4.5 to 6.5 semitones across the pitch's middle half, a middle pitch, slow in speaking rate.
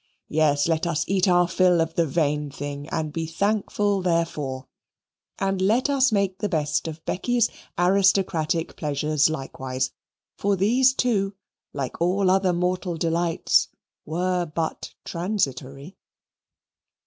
No: average, 4.1 semitones; medium, 170 Hz; slow, 125 wpm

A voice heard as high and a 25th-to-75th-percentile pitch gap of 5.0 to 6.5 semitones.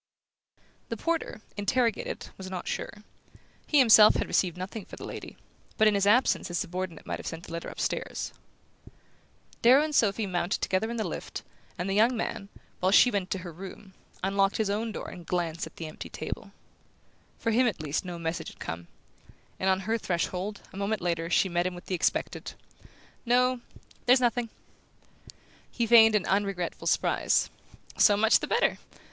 No: high, 195 Hz; average, 3.9 semitones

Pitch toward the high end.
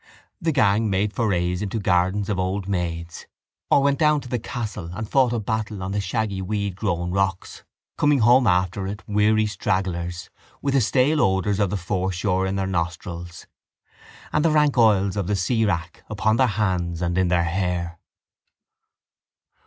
No: low, 100 Hz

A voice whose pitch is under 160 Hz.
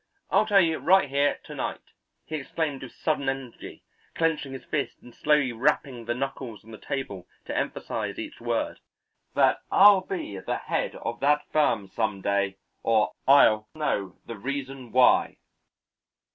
Yes: low, 135 Hz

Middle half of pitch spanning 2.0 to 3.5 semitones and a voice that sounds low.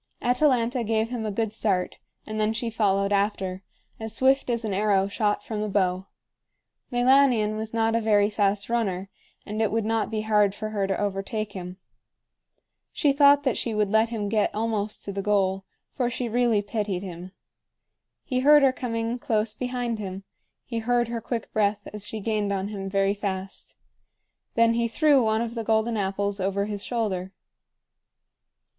No: narrow, 2.5 semitones; high, 215 Hz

